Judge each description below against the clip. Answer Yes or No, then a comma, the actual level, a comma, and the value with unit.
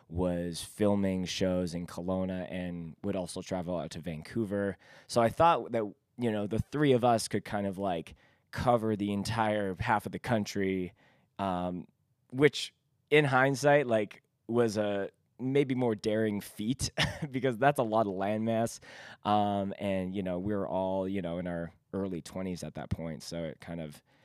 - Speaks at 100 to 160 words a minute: No, average, 175 wpm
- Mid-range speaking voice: No, low, 100 Hz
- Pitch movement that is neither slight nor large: Yes, average, 4.4 semitones